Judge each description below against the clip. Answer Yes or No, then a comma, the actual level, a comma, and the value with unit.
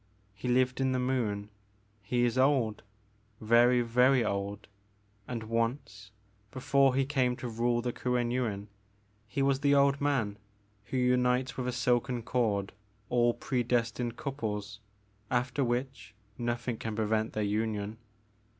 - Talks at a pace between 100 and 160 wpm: Yes, average, 140 wpm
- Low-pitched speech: Yes, low, 120 Hz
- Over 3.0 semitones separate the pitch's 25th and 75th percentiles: No, narrow, 2.6 semitones